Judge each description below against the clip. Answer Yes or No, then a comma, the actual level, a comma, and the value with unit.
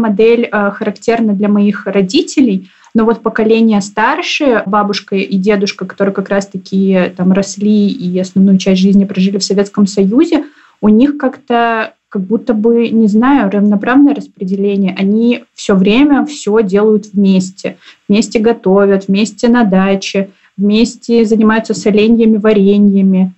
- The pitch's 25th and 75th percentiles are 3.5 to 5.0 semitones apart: No, average, 2.7 semitones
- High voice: Yes, high, 210 Hz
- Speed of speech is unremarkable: Yes, average, 130 wpm